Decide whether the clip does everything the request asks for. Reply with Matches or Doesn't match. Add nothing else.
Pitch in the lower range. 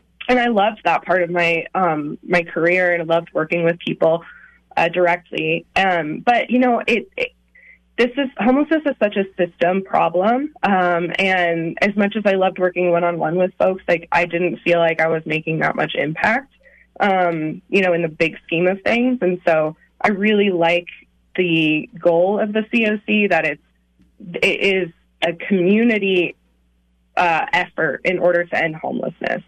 Doesn't match